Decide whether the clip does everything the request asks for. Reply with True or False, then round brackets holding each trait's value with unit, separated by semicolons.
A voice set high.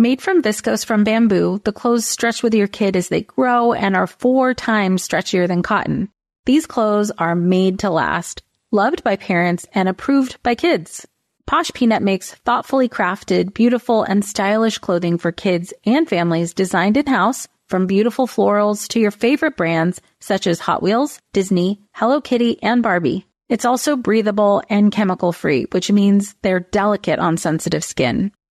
True (210 Hz)